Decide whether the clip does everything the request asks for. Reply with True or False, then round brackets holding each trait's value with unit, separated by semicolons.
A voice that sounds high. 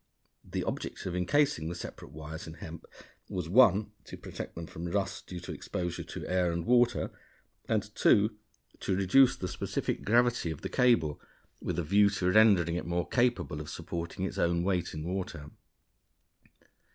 False (90 Hz)